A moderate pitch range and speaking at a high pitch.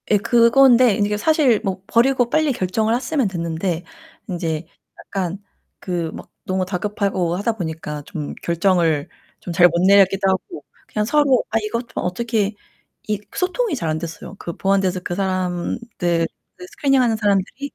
Yes: average, 4.9 semitones; high, 195 Hz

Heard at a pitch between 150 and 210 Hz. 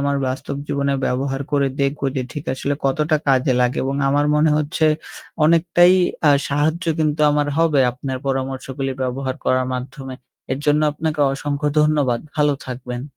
No: medium, 140 Hz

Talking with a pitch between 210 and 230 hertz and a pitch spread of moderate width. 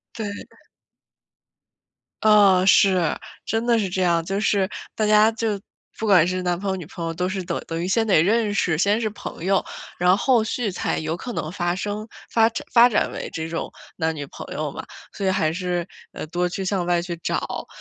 No: high, 190 Hz; average, 3.4 semitones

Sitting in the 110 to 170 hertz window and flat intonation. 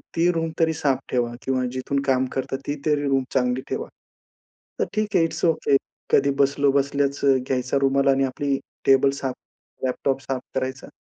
Yes: low, 135 Hz; narrow, 1.4 semitones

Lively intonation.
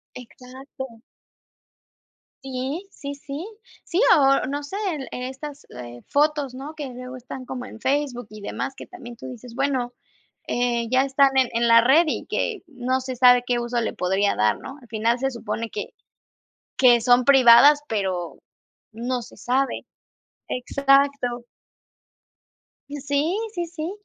No: average, 2.8 semitones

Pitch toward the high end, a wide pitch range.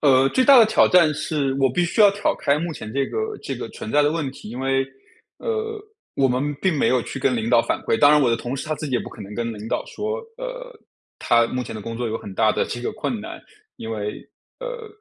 No: medium, 140 Hz; wide, 8.9 semitones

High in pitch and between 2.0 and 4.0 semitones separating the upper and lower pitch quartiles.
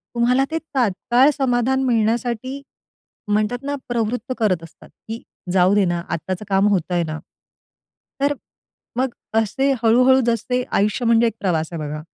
No: high, 225 Hz; average, 4.5 semitones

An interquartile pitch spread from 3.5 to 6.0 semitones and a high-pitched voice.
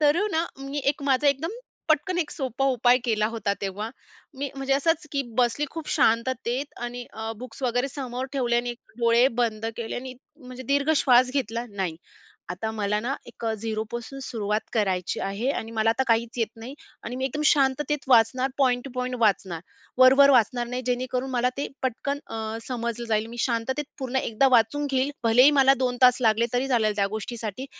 No: average, 3.1 semitones; high, 245 Hz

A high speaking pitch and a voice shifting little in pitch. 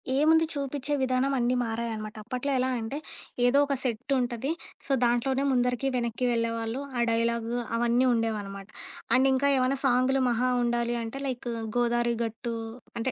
Yes: high, 245 Hz; narrow, 2.3 semitones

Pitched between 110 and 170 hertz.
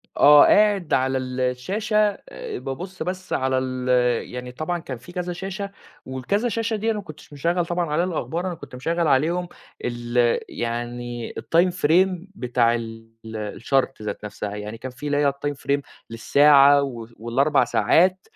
Yes: medium, 140 Hz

